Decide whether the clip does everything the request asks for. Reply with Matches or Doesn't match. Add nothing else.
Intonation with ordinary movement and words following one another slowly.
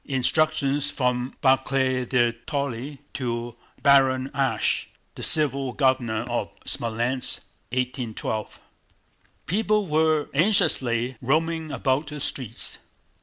Matches